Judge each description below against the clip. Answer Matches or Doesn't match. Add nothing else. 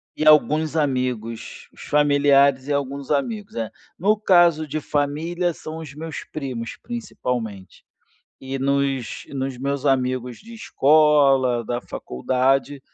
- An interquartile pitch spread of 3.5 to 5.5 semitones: Doesn't match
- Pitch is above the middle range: Doesn't match